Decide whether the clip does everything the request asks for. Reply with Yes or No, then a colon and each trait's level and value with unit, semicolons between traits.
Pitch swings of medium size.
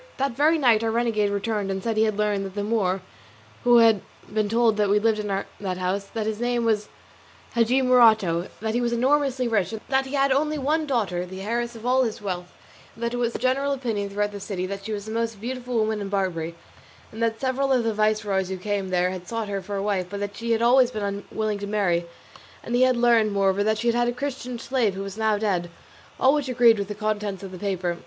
Yes: average, 3.2 semitones